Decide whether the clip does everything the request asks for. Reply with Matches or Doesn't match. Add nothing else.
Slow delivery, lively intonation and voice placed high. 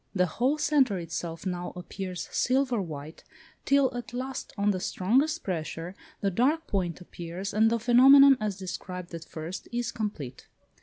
Doesn't match